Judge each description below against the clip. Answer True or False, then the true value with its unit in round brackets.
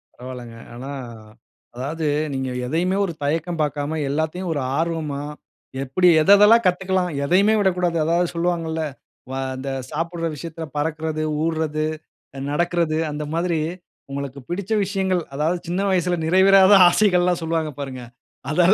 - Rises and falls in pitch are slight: False (3.2 semitones)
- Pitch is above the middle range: False (165 Hz)